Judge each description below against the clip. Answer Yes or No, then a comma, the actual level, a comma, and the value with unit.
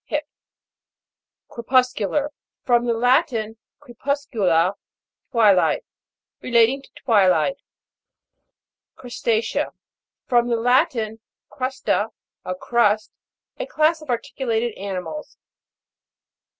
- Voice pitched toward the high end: Yes, high, 235 Hz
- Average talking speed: No, slow, 85 wpm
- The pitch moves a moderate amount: Yes, average, 3.4 semitones